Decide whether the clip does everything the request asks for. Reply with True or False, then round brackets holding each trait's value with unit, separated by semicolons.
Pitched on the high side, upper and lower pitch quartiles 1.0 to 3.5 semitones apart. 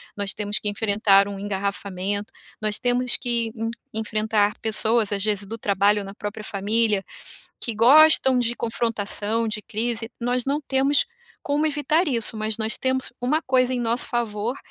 True (225 Hz; 3.0 semitones)